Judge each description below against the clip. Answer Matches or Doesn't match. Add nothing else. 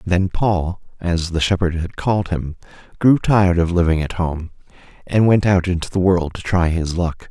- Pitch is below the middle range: Matches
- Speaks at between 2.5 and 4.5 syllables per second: Doesn't match